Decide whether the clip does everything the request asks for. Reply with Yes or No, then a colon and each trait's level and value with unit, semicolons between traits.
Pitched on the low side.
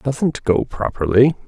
Yes: low, 125 Hz